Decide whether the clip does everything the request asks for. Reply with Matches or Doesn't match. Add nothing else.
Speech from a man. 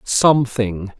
Matches